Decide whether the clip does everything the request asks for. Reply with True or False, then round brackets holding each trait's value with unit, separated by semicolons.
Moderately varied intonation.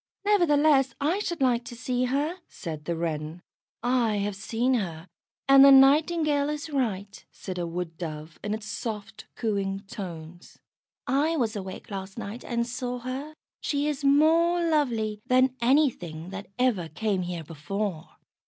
False (6.7 semitones)